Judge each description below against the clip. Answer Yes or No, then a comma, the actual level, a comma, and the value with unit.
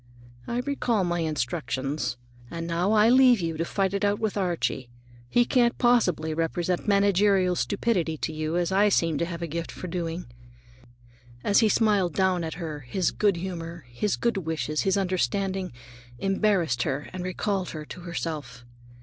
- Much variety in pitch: No, average, 3.7 semitones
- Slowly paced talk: No, average, 165 wpm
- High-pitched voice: No, medium, 180 Hz